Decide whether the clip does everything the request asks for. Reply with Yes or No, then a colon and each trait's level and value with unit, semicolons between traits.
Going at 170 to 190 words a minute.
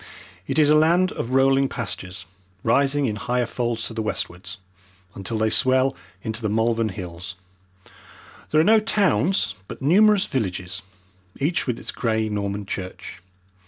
No: average, 150 wpm